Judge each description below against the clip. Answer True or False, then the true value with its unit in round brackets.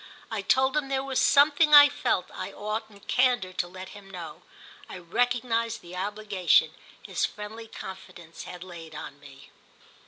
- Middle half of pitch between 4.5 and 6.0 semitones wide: True (5.4 semitones)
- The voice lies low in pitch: False (205 Hz)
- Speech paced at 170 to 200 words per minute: False (155 wpm)